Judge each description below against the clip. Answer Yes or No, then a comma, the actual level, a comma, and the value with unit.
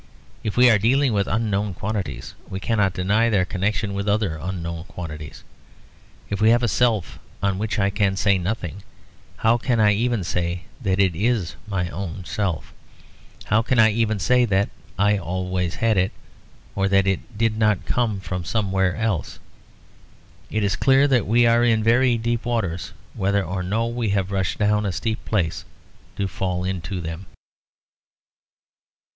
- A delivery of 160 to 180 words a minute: Yes, average, 165 wpm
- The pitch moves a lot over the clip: No, average, 3.3 semitones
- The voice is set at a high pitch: No, low, 100 Hz